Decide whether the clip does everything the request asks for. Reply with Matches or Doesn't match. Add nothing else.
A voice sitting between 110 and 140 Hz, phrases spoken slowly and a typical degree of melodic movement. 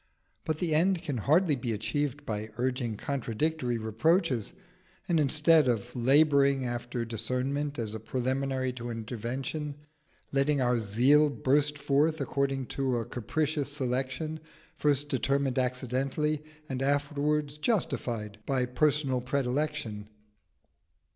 Matches